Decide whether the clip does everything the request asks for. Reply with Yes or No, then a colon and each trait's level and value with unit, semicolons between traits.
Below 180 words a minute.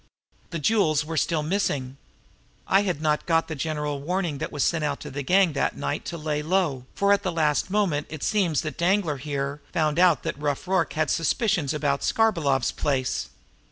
No: average, 195 wpm